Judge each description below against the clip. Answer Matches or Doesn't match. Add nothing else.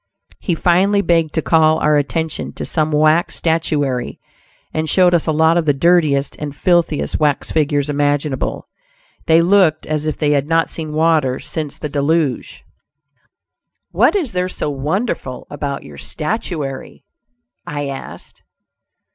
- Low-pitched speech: Doesn't match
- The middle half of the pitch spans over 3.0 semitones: Doesn't match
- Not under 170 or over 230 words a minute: Doesn't match